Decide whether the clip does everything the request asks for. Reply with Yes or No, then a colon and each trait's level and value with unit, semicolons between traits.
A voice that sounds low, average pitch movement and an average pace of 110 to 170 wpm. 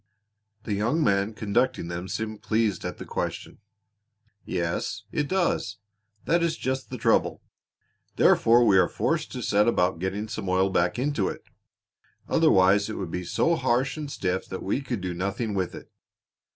Yes: low, 105 Hz; average, 4.9 semitones; average, 165 wpm